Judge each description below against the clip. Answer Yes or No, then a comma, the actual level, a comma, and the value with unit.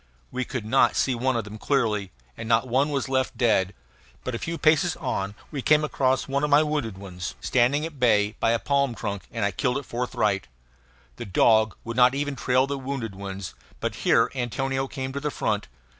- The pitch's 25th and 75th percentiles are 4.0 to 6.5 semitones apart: Yes, average, 4.3 semitones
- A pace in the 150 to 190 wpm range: No, fast, 205 wpm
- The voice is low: Yes, low, 125 Hz